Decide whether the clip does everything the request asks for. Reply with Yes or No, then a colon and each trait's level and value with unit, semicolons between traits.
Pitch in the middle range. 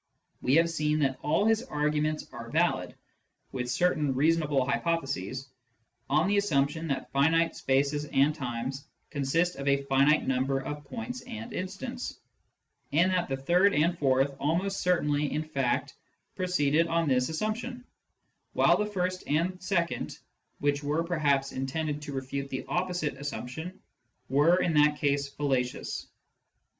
Yes: medium, 150 Hz